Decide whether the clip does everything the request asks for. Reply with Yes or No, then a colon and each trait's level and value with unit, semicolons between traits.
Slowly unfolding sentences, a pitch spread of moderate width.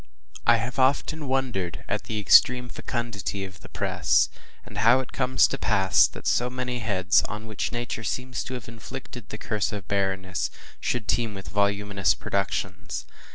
No: average, 165 wpm; average, 3.8 semitones